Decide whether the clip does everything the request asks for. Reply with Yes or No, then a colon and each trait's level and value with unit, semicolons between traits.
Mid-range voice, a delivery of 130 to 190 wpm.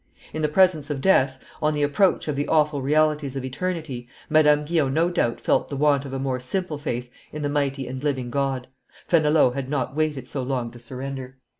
No: medium, 145 Hz; fast, 205 wpm